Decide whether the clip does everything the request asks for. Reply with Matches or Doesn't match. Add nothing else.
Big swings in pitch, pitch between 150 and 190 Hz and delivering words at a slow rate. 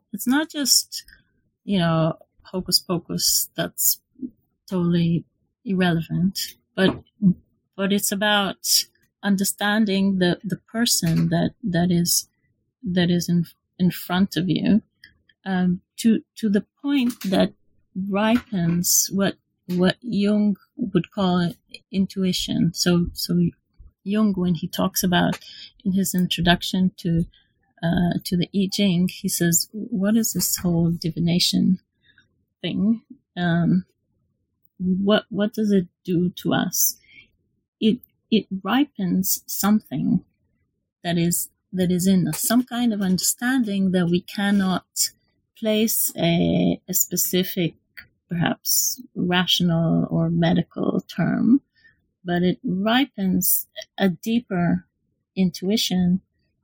Doesn't match